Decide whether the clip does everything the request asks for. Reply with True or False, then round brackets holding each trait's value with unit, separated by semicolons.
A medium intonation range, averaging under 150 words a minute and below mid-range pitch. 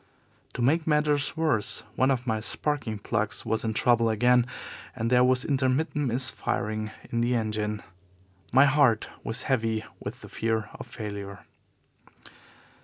True (3.3 semitones; 140 wpm; 120 Hz)